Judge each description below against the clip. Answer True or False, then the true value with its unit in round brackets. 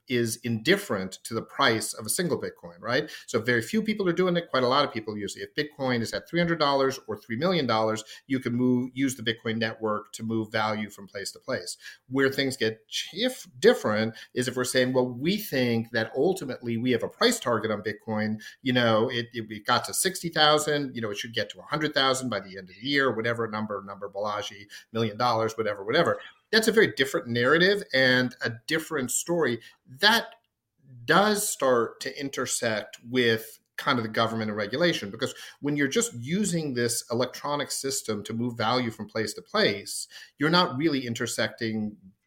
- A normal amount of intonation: True (4.3 semitones)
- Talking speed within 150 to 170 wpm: False (200 wpm)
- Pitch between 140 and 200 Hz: False (120 Hz)